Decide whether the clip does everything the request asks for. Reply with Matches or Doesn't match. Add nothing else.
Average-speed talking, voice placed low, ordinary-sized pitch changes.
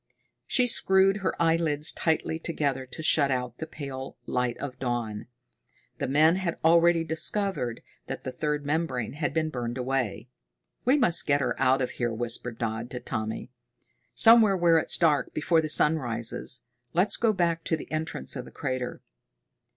Doesn't match